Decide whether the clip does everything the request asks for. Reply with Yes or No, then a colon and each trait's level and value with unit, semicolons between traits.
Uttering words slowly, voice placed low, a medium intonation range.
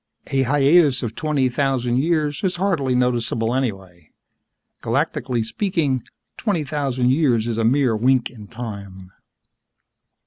Yes: slow, 125 wpm; low, 130 Hz; average, 4.0 semitones